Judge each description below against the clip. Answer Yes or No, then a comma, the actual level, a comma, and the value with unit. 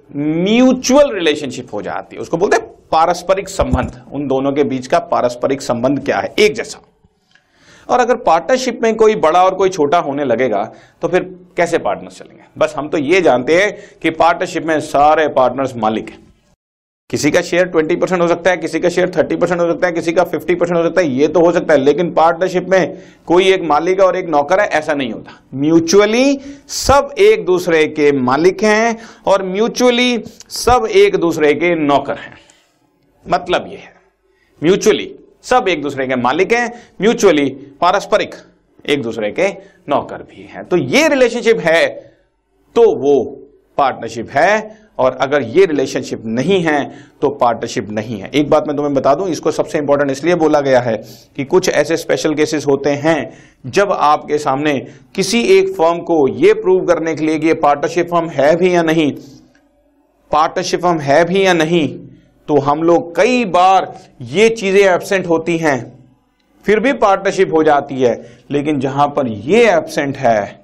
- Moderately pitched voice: Yes, medium, 175 Hz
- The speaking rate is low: No, average, 180 wpm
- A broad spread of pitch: Yes, wide, 6.2 semitones